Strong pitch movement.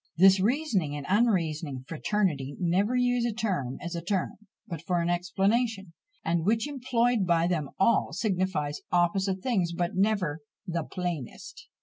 No: average, 4.2 semitones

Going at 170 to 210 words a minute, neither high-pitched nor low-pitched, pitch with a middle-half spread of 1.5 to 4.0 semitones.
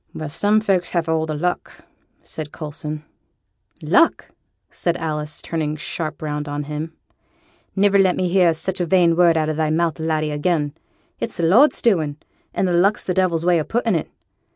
Yes: average, 175 wpm; medium, 165 Hz; average, 2.9 semitones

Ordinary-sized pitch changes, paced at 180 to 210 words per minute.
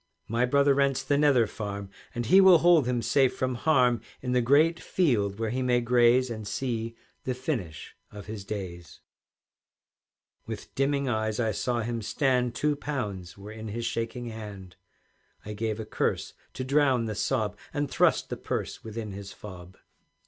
No: average, 3.9 semitones; average, 170 wpm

